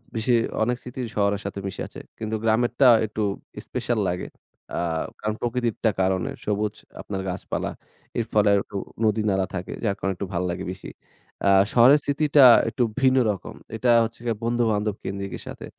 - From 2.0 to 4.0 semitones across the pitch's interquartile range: Yes, average, 3.3 semitones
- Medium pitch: No, low, 110 Hz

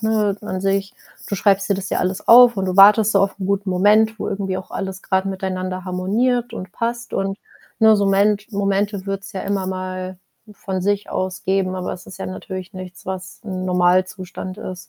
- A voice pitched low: No, high, 195 Hz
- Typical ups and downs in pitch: No, narrow, 1.5 semitones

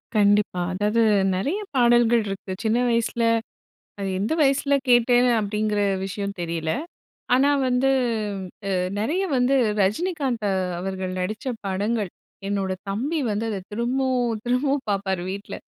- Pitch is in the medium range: No, high, 220 Hz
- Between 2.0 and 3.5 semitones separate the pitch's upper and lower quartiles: No, average, 4.0 semitones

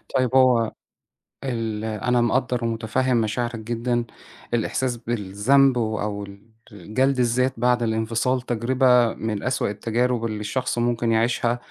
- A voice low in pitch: Yes, low, 120 Hz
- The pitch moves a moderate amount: No, narrow, 2.2 semitones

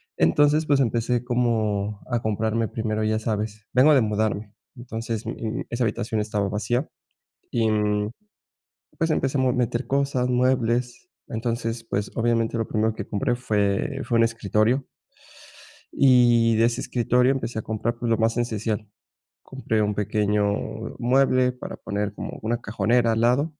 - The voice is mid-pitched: No, low, 115 Hz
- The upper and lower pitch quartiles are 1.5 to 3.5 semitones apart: Yes, narrow, 2.4 semitones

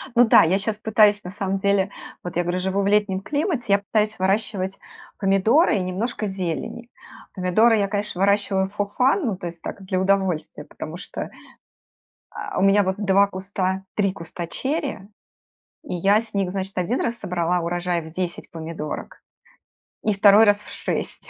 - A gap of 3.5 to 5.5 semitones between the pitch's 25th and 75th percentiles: No, narrow, 2.4 semitones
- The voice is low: No, high, 195 Hz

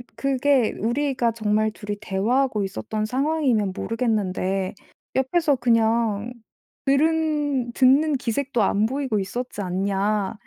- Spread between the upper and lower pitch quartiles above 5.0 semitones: No, average, 4.5 semitones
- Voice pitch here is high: Yes, high, 230 Hz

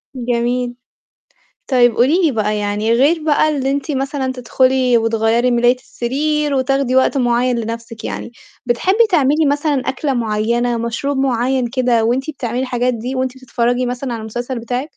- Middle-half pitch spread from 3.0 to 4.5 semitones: No, narrow, 2.4 semitones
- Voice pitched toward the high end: Yes, very high, 250 Hz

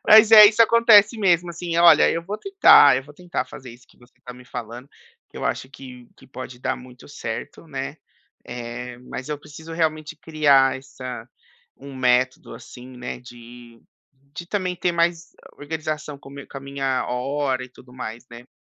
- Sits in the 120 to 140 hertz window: Yes, low, 135 Hz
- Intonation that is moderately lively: Yes, average, 4.8 semitones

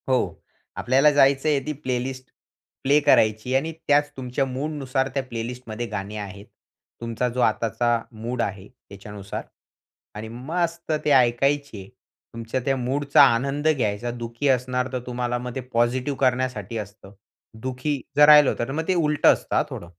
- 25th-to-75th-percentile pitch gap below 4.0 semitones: Yes, average, 3.2 semitones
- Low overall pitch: Yes, low, 125 Hz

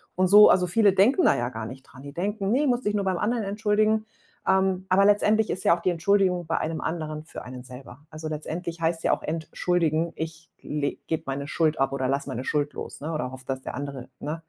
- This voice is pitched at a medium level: Yes, medium, 165 Hz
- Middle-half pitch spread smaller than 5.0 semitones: No, wide, 5.4 semitones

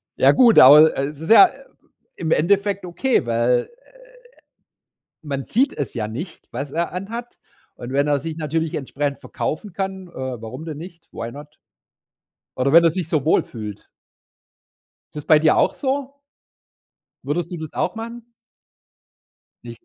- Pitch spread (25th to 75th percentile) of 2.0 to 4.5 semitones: No, wide, 5.6 semitones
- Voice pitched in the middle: Yes, medium, 155 Hz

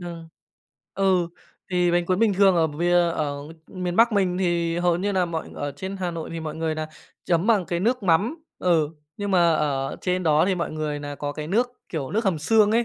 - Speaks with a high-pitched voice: No, medium, 175 Hz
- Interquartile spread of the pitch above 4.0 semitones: No, average, 3.2 semitones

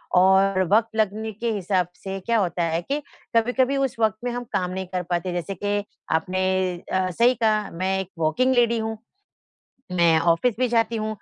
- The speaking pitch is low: No, high, 195 Hz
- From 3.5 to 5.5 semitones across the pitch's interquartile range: Yes, average, 3.9 semitones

